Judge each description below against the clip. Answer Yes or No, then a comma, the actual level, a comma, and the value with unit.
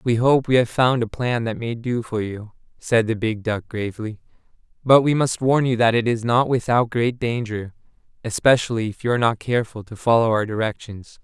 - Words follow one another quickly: Yes, fast, 210 wpm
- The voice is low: Yes, low, 115 Hz